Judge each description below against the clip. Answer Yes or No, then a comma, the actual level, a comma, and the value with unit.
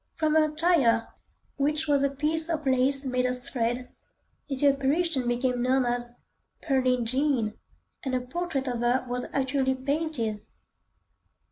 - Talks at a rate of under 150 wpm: Yes, average, 140 wpm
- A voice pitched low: No, very high, 265 Hz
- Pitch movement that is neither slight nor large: Yes, average, 3.0 semitones